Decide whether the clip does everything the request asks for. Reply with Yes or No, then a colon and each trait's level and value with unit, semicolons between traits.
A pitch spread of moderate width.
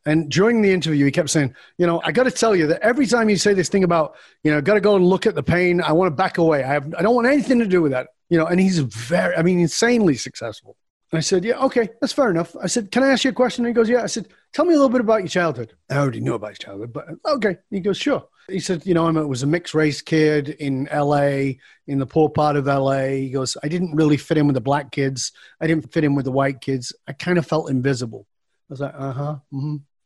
No: wide, 5.9 semitones